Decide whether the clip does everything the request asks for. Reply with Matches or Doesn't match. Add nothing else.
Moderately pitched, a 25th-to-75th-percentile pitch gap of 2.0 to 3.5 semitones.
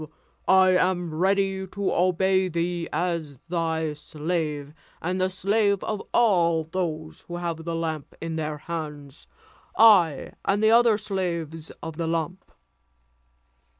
Matches